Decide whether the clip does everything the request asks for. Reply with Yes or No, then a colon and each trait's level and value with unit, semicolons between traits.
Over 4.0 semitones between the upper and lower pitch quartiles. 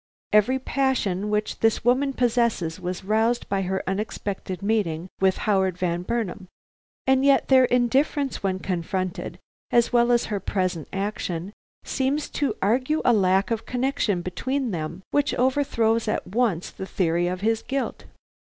Yes: average, 5.1 semitones